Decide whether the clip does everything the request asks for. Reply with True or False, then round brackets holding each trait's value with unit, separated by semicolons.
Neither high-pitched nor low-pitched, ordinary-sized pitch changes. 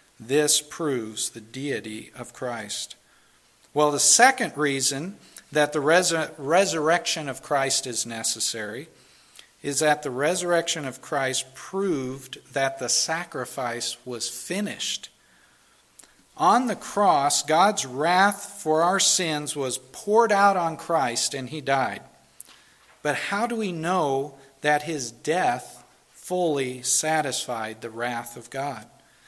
True (145 Hz; 4.6 semitones)